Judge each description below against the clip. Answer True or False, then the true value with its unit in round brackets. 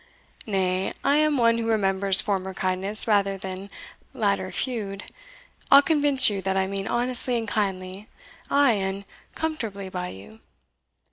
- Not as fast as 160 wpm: True (140 wpm)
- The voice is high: True (200 Hz)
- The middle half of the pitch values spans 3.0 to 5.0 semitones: True (3.4 semitones)